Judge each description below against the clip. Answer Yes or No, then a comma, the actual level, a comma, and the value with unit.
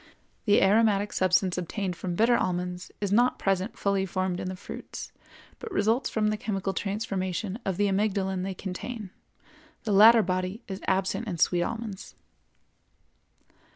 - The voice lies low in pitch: No, high, 195 Hz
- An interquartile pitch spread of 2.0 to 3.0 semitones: Yes, narrow, 2.4 semitones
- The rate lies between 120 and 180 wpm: Yes, average, 150 wpm